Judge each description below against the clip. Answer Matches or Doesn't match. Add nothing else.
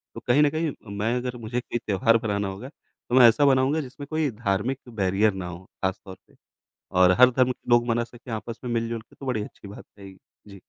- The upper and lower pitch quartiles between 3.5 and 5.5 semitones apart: Matches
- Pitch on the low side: Matches